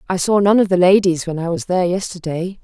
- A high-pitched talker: No, medium, 180 Hz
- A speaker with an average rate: No, fast, 250 wpm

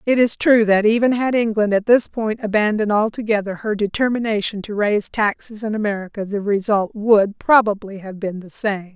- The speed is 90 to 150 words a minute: No, average, 180 wpm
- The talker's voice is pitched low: No, high, 210 Hz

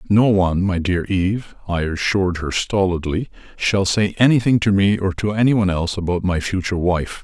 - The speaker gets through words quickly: No, average, 190 wpm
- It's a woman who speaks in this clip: No, male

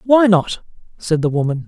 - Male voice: Yes, male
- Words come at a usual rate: Yes, average, 180 wpm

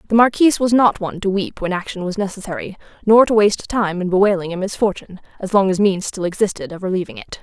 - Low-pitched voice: No, high, 195 Hz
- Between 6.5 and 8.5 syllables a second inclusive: Yes, 6.6 syllables/s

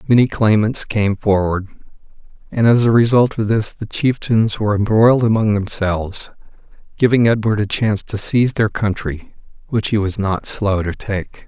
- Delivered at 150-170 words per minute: Yes, average, 160 wpm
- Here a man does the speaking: Yes, male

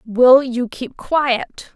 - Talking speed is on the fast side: No, slow, 135 wpm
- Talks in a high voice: Yes, very high, 250 Hz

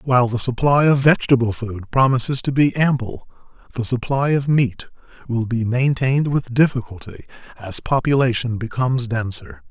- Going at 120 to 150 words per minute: Yes, average, 140 wpm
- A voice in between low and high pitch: No, low, 125 Hz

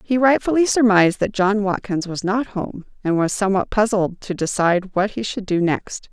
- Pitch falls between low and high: No, high, 200 Hz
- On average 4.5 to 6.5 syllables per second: Yes, 5.2 syllables/s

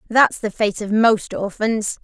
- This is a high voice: Yes, high, 215 Hz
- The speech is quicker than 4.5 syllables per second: No, 3.7 syllables/s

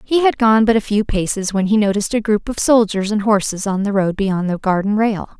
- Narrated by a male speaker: No, female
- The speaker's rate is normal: No, fast, 255 wpm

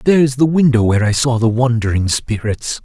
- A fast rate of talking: No, average, 190 wpm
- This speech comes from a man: Yes, male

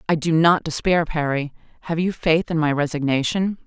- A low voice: No, medium, 160 Hz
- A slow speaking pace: No, average, 180 wpm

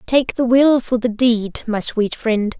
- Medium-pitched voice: No, high, 235 Hz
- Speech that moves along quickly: Yes, fast, 210 wpm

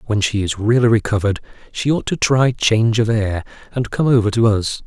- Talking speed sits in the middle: No, fast, 210 wpm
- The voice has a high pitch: No, low, 110 Hz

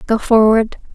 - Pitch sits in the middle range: No, high, 220 Hz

